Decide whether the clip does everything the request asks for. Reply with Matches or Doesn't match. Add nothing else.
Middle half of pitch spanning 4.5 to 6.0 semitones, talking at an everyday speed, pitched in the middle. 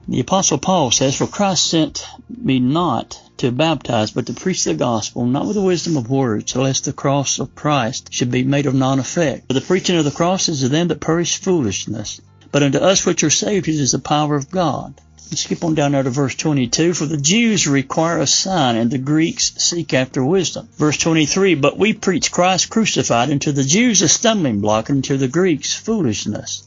Doesn't match